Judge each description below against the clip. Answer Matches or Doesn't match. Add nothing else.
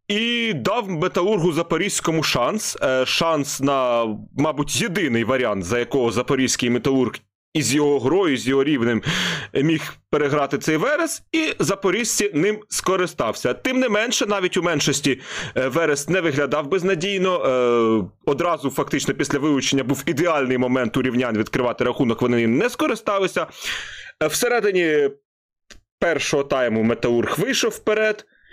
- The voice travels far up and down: Matches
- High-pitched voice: Doesn't match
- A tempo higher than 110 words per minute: Matches